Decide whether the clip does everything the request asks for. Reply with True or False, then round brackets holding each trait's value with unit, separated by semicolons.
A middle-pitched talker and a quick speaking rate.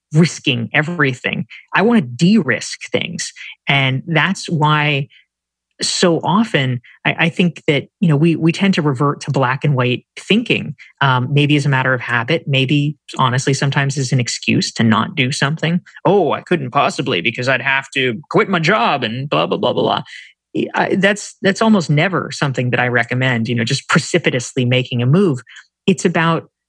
False (145 Hz; 180 wpm)